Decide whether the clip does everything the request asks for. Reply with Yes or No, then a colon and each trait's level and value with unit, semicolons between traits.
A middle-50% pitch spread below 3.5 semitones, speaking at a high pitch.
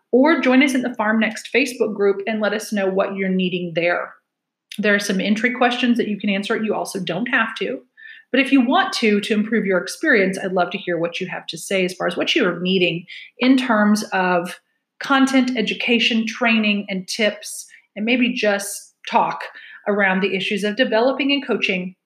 No: average, 4.2 semitones; high, 210 Hz